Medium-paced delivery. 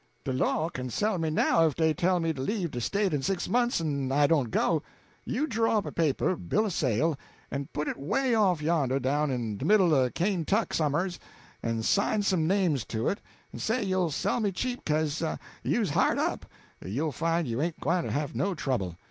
No: fast, 210 wpm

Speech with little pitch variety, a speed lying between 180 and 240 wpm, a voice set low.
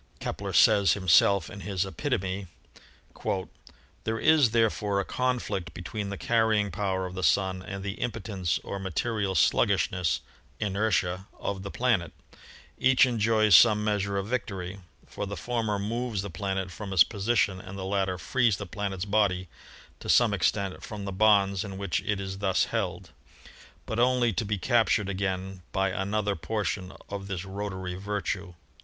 No: narrow, 2.2 semitones; average, 160 wpm; low, 100 Hz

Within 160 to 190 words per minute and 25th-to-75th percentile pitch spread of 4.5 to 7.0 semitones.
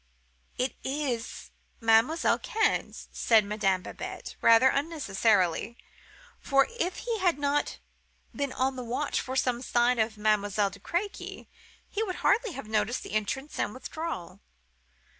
No: slow, 135 wpm; wide, 5.5 semitones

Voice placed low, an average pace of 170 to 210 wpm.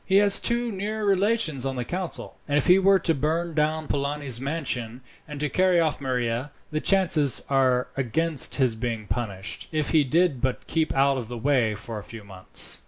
No: medium, 145 Hz; average, 195 wpm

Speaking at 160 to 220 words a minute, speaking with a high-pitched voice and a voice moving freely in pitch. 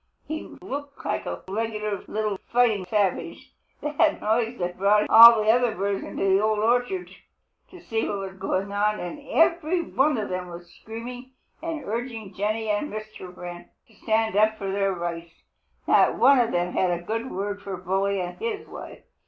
No: average, 180 wpm; high, 215 Hz; average, 3.7 semitones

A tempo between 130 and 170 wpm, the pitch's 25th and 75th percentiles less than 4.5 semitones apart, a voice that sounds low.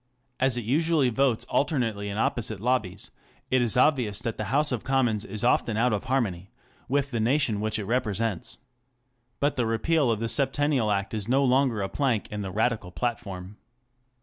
No: average, 180 wpm; average, 4.1 semitones; low, 115 Hz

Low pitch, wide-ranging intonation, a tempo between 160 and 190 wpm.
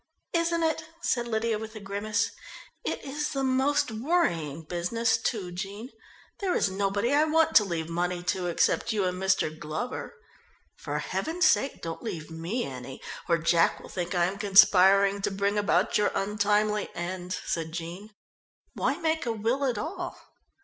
No: high, 205 Hz; wide, 5.7 semitones; average, 165 wpm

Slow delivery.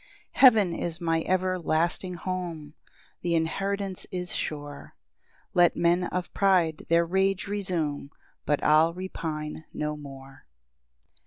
Yes: slow, 115 wpm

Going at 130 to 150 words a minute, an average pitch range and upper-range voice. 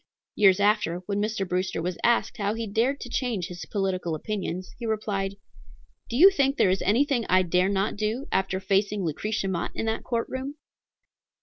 No: average, 185 wpm; average, 3.5 semitones; high, 205 Hz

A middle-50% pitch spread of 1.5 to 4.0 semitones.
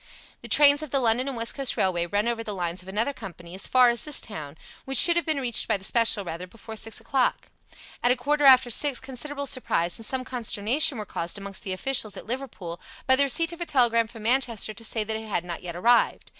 No: average, 5.0 semitones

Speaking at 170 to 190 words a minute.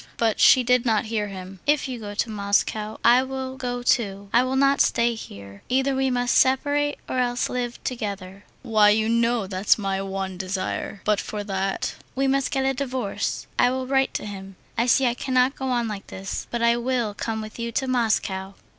No: fast, 205 wpm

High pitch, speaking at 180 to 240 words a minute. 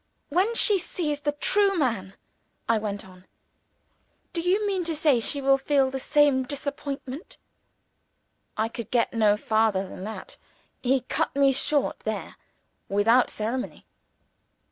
No: very high, 270 Hz; average, 145 wpm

